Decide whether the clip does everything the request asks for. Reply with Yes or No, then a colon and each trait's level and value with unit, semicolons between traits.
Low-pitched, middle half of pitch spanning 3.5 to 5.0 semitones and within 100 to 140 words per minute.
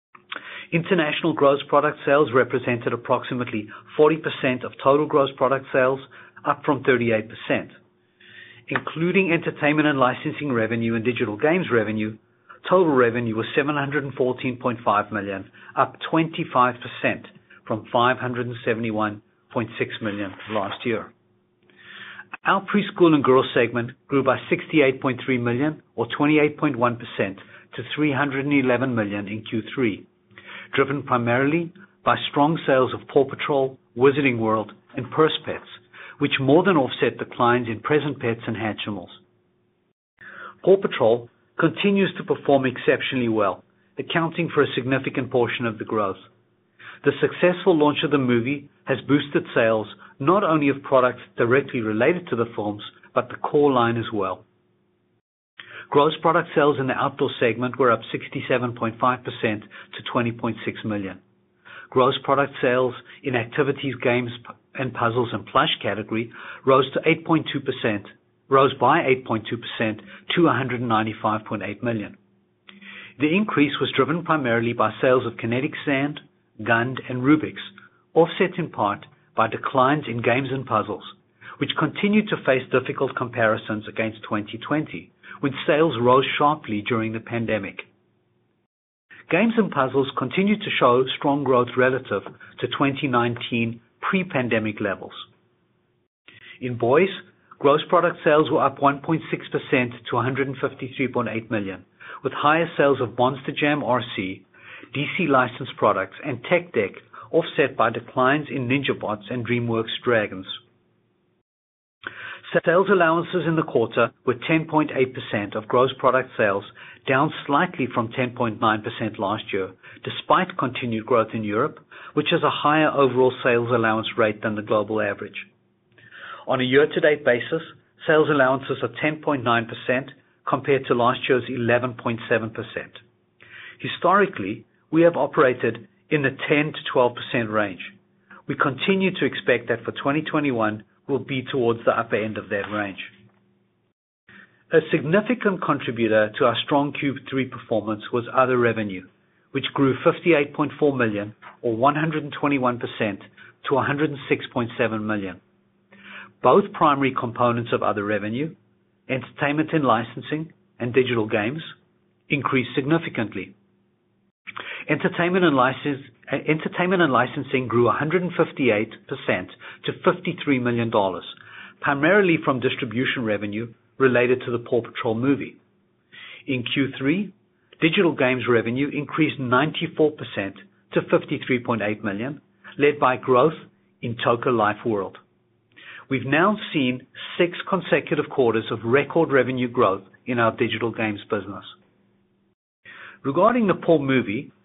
Yes: low, 130 Hz; average, 4.3 semitones; slow, 135 wpm